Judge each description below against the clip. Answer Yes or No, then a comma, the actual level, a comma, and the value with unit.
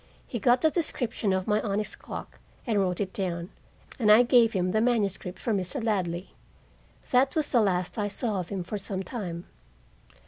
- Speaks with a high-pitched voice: Yes, high, 205 Hz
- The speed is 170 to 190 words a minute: Yes, average, 185 wpm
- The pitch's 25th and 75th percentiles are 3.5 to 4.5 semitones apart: Yes, average, 4.1 semitones